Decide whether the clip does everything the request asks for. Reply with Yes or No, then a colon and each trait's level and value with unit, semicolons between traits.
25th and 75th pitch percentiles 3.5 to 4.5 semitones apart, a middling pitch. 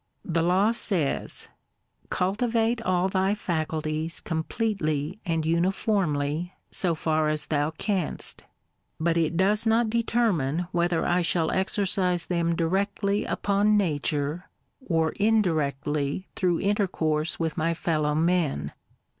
Yes: average, 4.0 semitones; medium, 170 Hz